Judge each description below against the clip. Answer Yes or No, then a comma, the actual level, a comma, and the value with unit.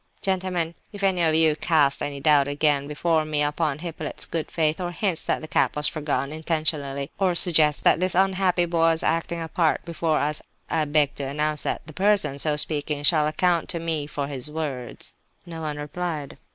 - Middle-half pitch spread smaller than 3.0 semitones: Yes, narrow, 2.5 semitones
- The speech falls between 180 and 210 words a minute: Yes, average, 200 wpm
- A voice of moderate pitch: Yes, medium, 155 Hz